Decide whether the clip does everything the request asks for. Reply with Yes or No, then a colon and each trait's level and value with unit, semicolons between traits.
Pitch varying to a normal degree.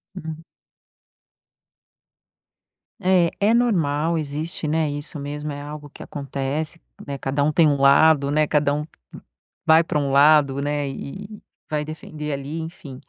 No: narrow, 2.0 semitones